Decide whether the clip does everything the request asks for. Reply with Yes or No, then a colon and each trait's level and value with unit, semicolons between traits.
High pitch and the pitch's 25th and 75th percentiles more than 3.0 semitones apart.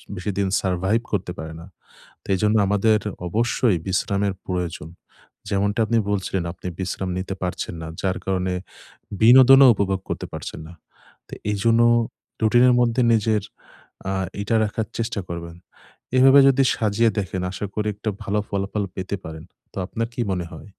No: low, 100 Hz; average, 3.4 semitones